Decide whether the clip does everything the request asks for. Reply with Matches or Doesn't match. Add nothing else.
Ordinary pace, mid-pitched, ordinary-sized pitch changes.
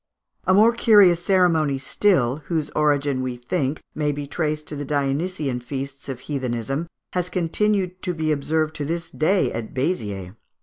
Matches